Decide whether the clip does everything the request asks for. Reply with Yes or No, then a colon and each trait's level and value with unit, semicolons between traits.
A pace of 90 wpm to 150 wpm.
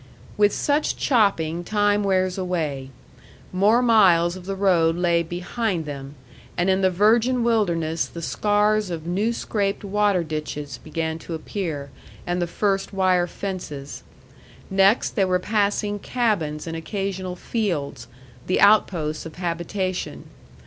Yes: slow, 135 wpm